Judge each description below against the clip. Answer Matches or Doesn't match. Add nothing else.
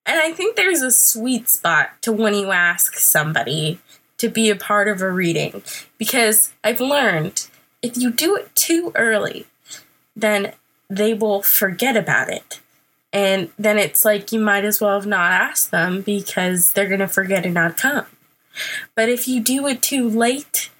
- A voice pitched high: Matches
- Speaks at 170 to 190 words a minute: Matches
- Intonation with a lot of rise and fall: Doesn't match